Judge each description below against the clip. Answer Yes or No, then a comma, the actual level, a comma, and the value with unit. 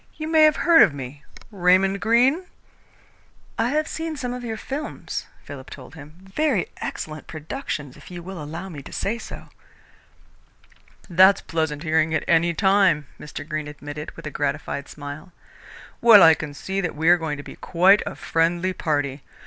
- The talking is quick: No, average, 175 wpm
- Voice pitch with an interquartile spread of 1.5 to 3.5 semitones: No, wide, 5.5 semitones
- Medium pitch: Yes, medium, 170 Hz